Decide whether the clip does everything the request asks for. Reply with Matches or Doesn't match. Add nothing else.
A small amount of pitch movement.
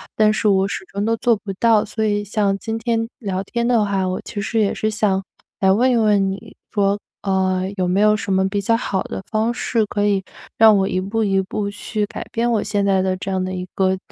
Matches